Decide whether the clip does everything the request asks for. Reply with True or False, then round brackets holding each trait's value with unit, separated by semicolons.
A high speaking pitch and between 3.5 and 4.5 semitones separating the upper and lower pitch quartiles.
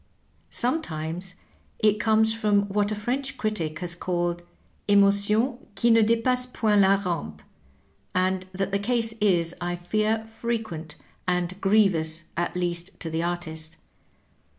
True (200 Hz; 4.1 semitones)